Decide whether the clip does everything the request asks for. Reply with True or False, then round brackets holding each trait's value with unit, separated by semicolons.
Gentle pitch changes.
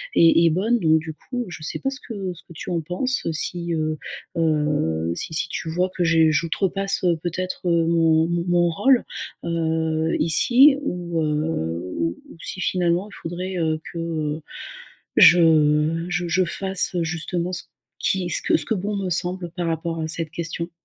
True (2.2 semitones)